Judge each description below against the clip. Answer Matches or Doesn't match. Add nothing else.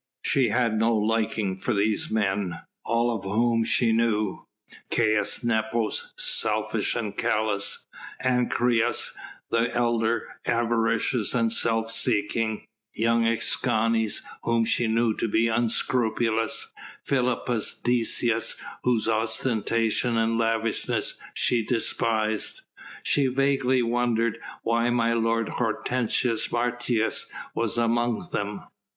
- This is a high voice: Doesn't match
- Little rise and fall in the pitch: Matches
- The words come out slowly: Matches